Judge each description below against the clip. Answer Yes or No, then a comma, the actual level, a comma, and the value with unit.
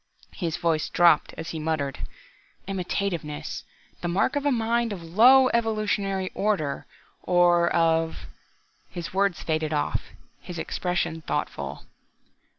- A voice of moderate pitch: Yes, medium, 175 Hz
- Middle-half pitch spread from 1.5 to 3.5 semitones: No, average, 4.0 semitones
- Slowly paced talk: Yes, slow, 125 wpm